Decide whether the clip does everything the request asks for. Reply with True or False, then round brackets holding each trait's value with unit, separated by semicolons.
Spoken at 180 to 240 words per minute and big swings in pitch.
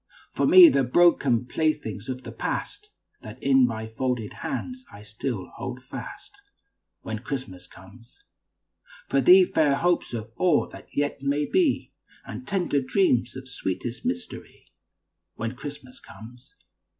False (140 wpm; 5.7 semitones)